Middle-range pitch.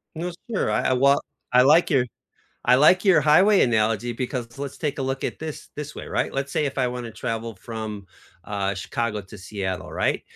No: low, 125 Hz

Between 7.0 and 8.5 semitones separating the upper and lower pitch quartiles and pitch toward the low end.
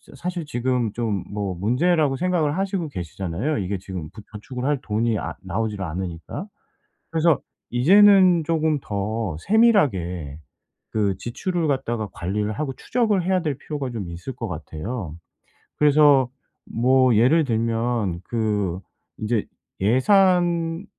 Yes: wide, 7.8 semitones; low, 120 Hz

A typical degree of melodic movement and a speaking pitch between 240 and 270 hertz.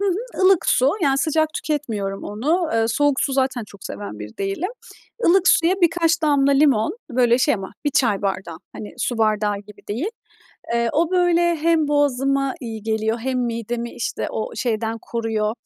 No: wide, 6.2 semitones; very high, 255 Hz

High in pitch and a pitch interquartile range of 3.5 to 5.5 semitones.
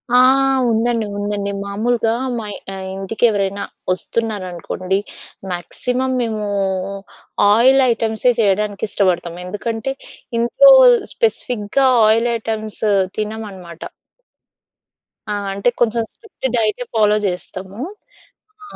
No: high, 215 Hz; average, 2.8 semitones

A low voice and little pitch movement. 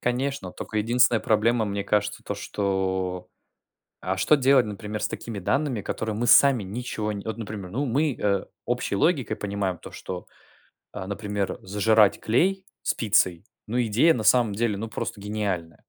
No: low, 105 Hz; average, 3.4 semitones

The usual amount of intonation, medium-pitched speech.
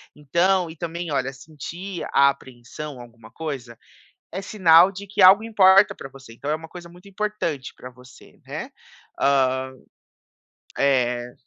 No: wide, 5.9 semitones; medium, 155 Hz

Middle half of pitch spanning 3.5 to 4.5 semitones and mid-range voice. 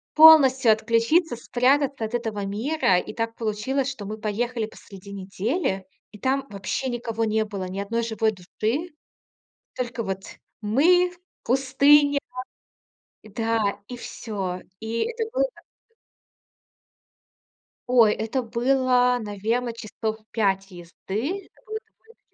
No: average, 4.0 semitones; high, 230 Hz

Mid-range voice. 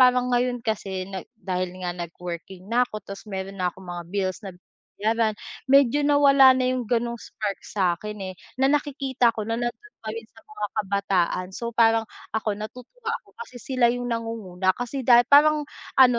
No: high, 225 Hz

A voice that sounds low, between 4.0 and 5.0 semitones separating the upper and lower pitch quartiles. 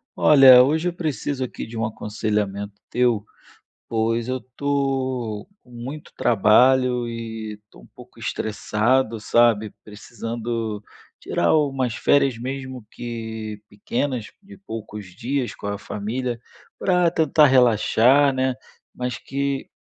No: low, 120 Hz; average, 3.4 semitones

